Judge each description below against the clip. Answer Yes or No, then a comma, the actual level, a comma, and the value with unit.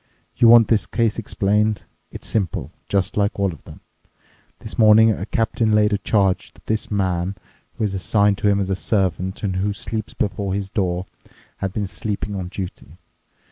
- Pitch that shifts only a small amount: Yes, narrow, 2.1 semitones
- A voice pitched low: Yes, low, 100 Hz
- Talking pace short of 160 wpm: No, average, 180 wpm